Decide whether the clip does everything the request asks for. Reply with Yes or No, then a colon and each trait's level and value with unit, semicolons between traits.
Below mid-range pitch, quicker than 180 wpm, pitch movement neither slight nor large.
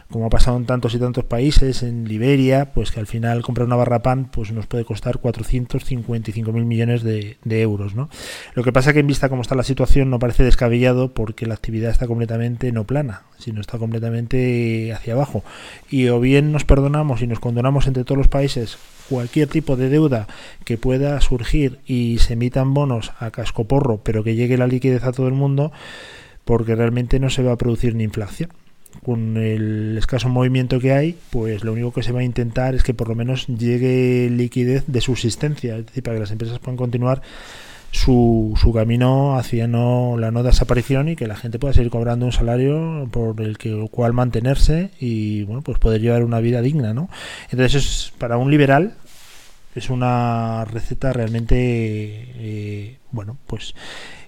No: low, 120 Hz; fast, 190 wpm; narrow, 2.2 semitones